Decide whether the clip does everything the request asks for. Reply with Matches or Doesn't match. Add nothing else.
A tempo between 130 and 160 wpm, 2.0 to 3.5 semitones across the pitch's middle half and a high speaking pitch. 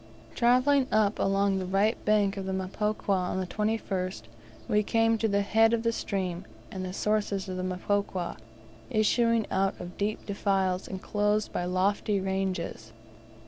Matches